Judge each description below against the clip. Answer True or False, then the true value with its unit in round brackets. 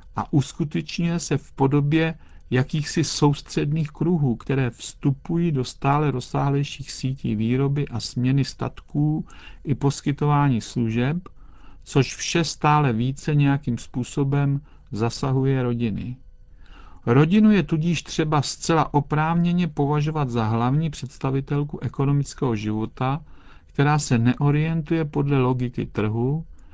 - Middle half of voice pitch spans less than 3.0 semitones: False (3.3 semitones)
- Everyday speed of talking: False (105 wpm)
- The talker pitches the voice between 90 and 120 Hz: False (140 Hz)